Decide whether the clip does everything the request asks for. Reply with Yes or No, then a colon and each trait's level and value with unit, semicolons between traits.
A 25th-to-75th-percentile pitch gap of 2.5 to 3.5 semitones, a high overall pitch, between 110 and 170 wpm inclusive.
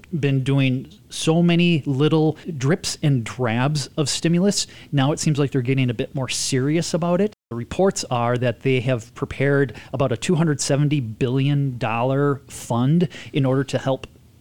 No: average, 3.2 semitones; low, 135 Hz; average, 160 wpm